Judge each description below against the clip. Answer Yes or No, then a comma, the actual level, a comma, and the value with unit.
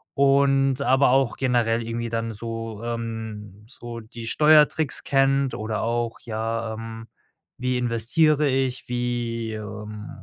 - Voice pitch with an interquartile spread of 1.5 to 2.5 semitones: No, average, 2.9 semitones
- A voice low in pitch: Yes, low, 115 Hz